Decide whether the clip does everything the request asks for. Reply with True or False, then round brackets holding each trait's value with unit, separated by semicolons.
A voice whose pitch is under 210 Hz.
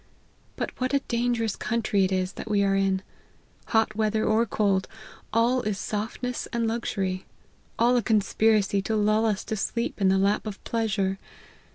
False (215 Hz)